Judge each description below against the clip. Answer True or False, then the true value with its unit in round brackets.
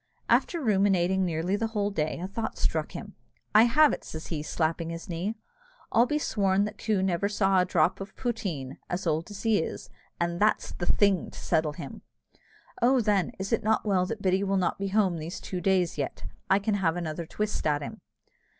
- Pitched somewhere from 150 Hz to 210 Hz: True (190 Hz)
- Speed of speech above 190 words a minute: True (205 wpm)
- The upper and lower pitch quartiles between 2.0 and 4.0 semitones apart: True (3.5 semitones)